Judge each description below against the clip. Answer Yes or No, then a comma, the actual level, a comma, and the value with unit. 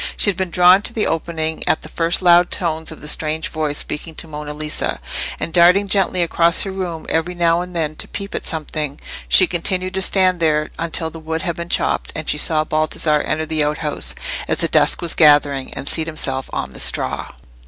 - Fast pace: Yes, fast, 215 wpm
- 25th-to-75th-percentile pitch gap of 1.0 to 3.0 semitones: Yes, narrow, 2.4 semitones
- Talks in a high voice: No, medium, 160 Hz